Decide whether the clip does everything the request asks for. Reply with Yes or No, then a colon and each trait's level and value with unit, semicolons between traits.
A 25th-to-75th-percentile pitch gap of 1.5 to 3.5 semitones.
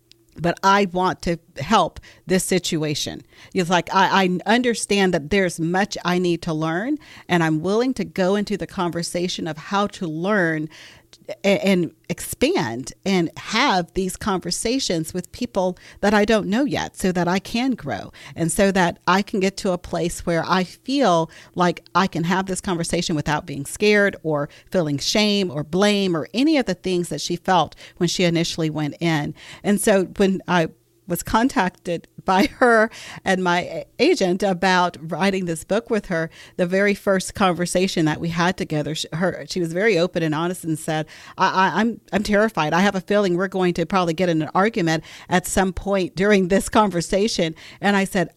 Yes: average, 2.9 semitones